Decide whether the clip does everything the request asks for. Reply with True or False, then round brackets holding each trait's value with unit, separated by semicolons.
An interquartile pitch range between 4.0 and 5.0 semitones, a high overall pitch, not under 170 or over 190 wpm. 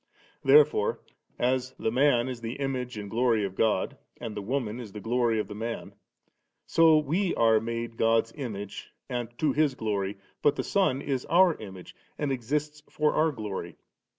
False (4.7 semitones; 120 Hz; 175 wpm)